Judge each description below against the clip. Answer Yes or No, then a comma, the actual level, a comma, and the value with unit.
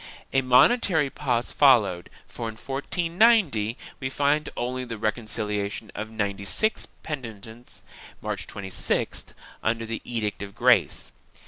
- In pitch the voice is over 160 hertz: No, low, 120 Hz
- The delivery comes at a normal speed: No, slow, 120 wpm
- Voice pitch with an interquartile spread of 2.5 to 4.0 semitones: No, average, 4.4 semitones